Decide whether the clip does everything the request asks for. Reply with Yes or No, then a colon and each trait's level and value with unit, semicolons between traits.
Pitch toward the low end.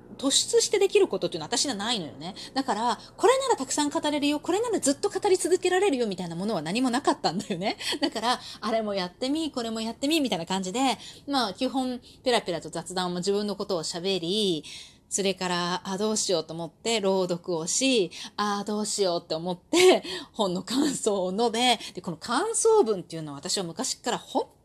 No: high, 220 Hz